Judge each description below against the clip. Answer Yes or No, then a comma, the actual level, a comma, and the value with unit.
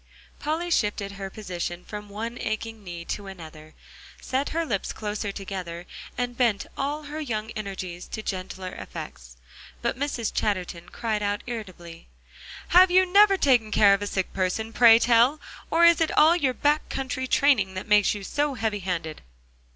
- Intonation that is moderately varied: No, wide, 5.9 semitones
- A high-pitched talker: Yes, high, 215 Hz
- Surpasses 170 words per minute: No, average, 165 wpm